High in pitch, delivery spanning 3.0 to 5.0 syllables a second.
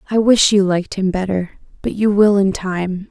Yes: high, 195 Hz; 4.9 syllables/s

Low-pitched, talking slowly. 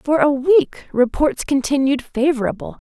No: very high, 270 Hz; slow, 125 wpm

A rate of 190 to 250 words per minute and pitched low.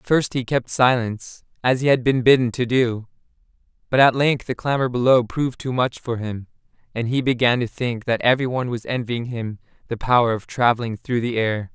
Yes: fast, 205 wpm; low, 120 Hz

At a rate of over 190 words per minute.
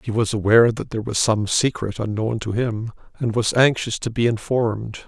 Yes: average, 200 wpm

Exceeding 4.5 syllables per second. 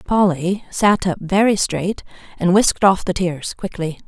No: 4.4 syllables/s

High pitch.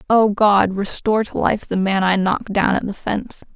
Yes: high, 200 Hz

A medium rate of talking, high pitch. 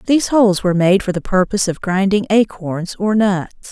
Yes: average, 195 wpm; high, 195 Hz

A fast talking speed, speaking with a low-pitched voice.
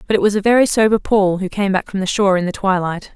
No: fast, 305 wpm; high, 195 Hz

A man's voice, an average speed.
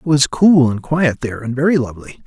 No: male; fast, 240 wpm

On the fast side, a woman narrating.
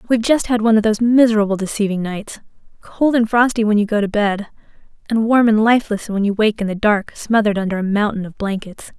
Yes: fast, 215 wpm; female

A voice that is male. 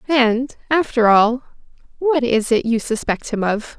No: female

